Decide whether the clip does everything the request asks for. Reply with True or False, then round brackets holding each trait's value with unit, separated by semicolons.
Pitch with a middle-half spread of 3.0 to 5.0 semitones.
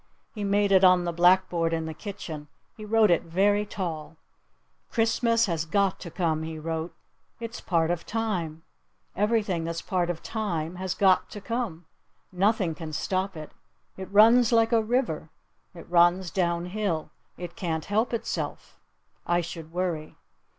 True (4.0 semitones)